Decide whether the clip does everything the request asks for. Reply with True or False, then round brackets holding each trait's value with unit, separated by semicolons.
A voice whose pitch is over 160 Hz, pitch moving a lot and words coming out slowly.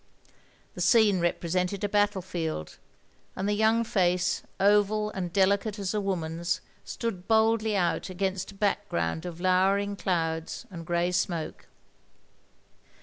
False (190 Hz; 2.8 semitones; 130 wpm)